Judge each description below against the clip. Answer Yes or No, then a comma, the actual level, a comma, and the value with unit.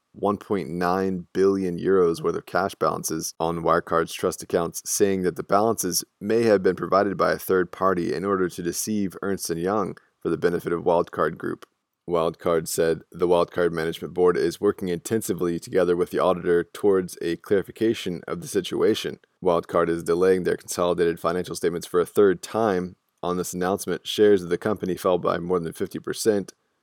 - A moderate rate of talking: Yes, average, 170 wpm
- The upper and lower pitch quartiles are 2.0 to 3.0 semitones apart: Yes, narrow, 2.4 semitones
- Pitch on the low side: Yes, very low, 90 Hz